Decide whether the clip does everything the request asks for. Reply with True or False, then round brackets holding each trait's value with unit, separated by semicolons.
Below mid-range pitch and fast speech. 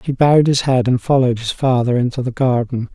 True (125 Hz; 225 wpm)